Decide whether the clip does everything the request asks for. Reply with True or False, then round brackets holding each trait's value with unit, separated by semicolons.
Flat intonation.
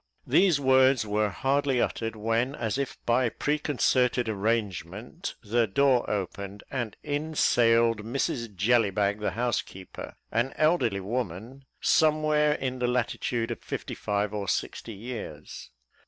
False (4.1 semitones)